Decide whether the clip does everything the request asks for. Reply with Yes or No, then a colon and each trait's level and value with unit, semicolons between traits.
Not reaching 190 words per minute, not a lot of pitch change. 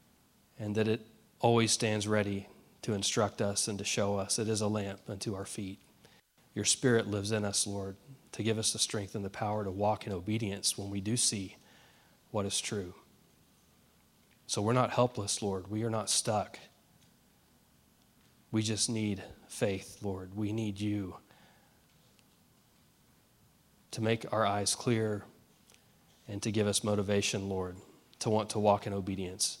Yes: average, 160 wpm; narrow, 1.8 semitones